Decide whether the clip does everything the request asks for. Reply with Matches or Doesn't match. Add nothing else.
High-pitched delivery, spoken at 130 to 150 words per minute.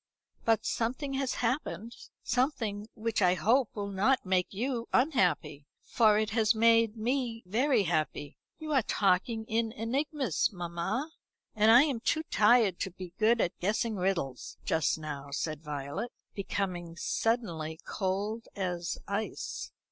Matches